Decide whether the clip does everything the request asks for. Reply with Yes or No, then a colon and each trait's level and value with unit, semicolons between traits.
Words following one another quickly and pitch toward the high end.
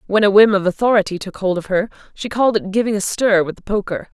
Yes: fast, 260 wpm; high, 200 Hz